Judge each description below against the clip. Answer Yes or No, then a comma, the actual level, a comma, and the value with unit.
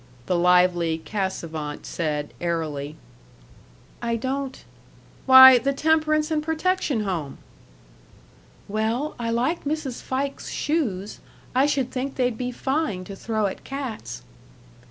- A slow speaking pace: Yes, slow, 120 wpm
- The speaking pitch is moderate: No, high, 235 Hz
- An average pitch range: No, wide, 7.4 semitones